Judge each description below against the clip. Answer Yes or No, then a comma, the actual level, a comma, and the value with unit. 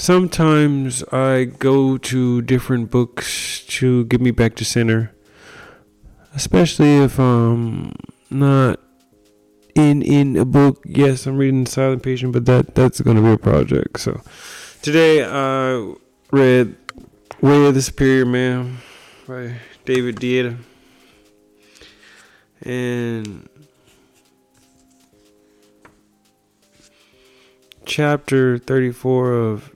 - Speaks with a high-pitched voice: No, low, 125 Hz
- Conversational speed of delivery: No, slow, 100 wpm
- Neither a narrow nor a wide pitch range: Yes, average, 3.1 semitones